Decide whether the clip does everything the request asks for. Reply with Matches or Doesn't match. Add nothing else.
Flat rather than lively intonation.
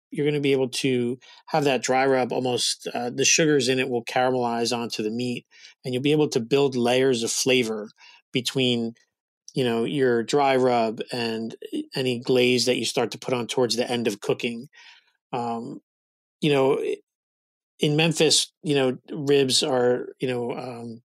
Matches